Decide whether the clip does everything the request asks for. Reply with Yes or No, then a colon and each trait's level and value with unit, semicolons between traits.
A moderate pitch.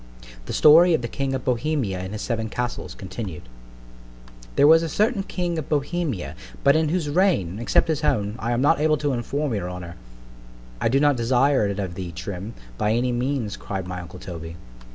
No: low, 125 Hz